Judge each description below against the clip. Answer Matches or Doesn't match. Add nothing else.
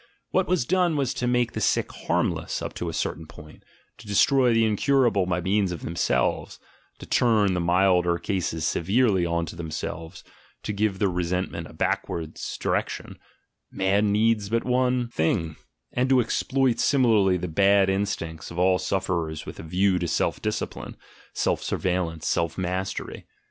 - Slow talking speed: Doesn't match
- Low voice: Matches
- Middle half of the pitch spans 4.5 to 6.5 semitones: Matches